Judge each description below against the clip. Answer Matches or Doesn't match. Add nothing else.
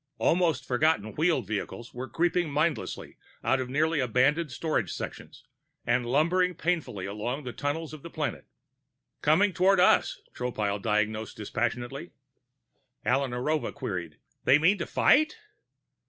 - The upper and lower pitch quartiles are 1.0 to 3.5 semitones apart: Doesn't match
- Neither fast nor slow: Doesn't match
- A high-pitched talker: Doesn't match